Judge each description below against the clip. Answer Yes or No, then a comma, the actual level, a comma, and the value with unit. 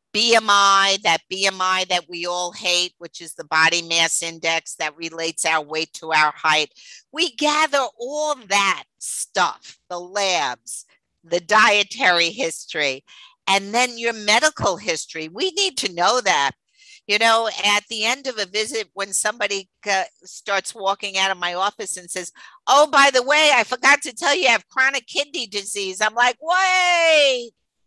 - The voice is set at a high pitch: Yes, high, 200 Hz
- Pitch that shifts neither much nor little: No, wide, 6.4 semitones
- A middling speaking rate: Yes, average, 160 wpm